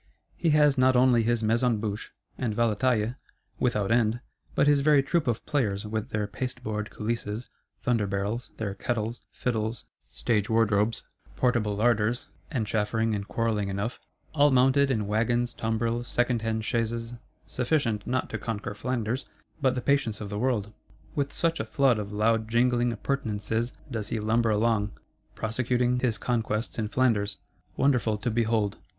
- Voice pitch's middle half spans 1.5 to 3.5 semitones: Yes, average, 2.7 semitones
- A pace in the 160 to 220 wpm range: No, average, 150 wpm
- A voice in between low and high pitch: No, low, 115 Hz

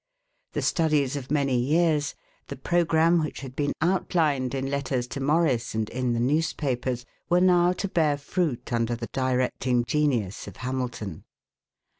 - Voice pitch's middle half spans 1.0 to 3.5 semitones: No, average, 4.3 semitones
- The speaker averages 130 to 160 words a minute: Yes, average, 150 wpm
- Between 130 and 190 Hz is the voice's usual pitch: Yes, medium, 140 Hz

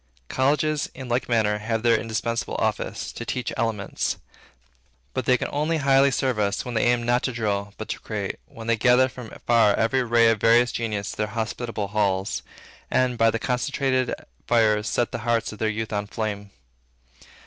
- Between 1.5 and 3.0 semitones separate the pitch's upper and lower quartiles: Yes, narrow, 2.6 semitones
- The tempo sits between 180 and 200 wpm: Yes, average, 185 wpm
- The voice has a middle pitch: No, low, 115 Hz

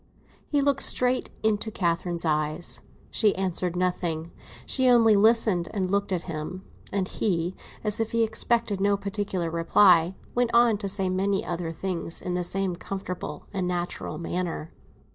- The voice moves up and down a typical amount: Yes, average, 3.3 semitones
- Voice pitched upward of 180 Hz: Yes, high, 190 Hz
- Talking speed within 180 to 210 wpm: No, average, 155 wpm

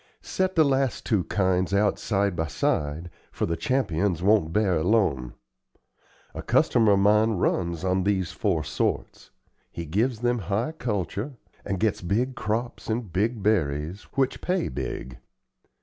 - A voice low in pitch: Yes, low, 100 Hz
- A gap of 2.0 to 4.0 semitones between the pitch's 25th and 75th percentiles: No, average, 4.7 semitones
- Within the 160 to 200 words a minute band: No, average, 150 wpm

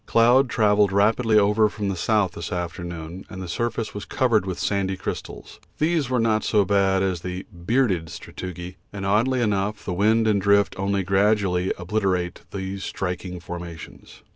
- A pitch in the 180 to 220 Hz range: No, low, 100 Hz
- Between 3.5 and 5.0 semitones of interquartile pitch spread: No, average, 3.0 semitones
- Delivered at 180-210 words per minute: No, average, 165 wpm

